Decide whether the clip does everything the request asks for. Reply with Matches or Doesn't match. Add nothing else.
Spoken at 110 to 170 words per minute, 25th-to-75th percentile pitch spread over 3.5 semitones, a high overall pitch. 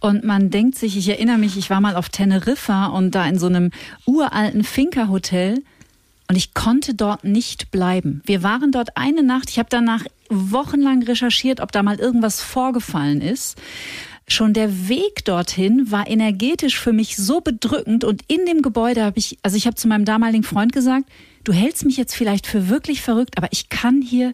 Doesn't match